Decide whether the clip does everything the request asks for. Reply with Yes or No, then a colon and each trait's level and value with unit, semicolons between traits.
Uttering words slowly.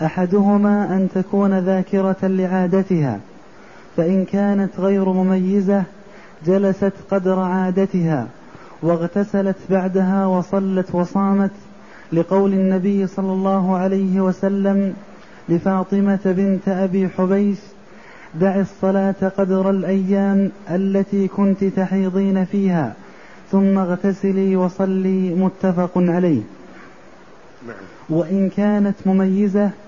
No: average, 85 wpm